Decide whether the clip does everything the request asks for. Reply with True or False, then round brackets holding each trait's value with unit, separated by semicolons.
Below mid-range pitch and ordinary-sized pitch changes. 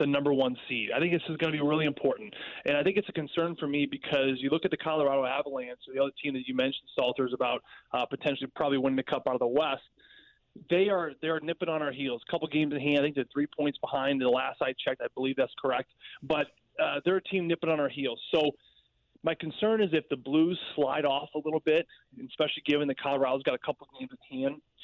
False (145 Hz; 3.3 semitones)